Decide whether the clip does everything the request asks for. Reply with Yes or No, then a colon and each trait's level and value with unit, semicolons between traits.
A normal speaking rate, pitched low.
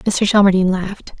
No: average, 150 wpm; high, 195 Hz